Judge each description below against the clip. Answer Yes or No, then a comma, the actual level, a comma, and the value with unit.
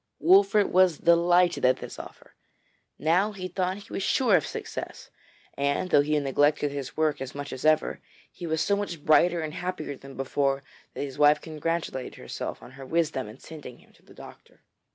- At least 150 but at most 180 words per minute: No, average, 190 wpm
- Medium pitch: Yes, medium, 155 Hz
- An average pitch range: Yes, average, 4.0 semitones